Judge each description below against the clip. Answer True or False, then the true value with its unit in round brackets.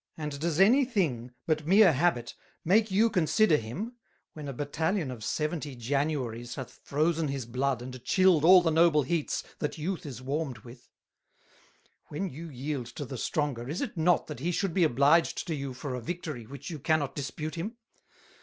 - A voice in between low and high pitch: True (150 Hz)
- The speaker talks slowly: False (180 wpm)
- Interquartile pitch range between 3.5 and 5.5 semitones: True (4.5 semitones)